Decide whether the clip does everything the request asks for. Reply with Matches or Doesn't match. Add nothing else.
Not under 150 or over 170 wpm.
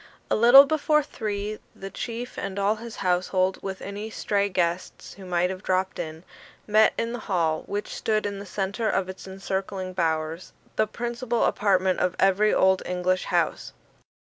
Matches